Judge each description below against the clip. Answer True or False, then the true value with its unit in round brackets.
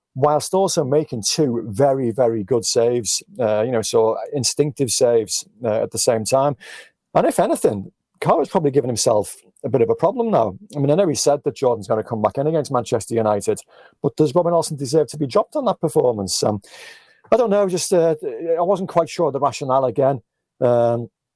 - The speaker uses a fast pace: True (210 wpm)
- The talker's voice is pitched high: False (140 Hz)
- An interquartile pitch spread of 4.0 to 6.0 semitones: True (5.4 semitones)